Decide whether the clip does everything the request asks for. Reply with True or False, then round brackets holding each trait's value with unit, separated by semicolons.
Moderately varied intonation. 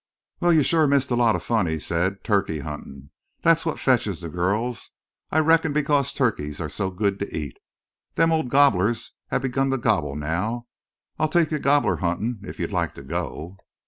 False (8.2 semitones)